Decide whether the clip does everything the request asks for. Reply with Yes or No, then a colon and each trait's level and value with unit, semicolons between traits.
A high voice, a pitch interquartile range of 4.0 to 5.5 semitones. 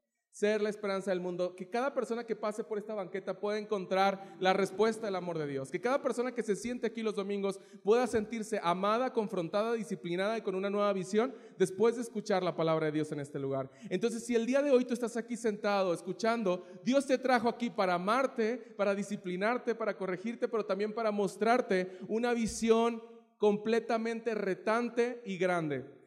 No: high, 210 Hz; average, 3.3 semitones